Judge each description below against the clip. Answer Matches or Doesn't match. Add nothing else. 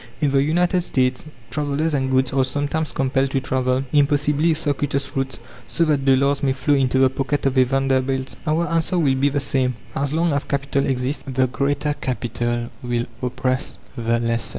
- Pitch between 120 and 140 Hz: Matches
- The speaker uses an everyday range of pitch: Doesn't match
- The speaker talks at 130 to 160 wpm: Doesn't match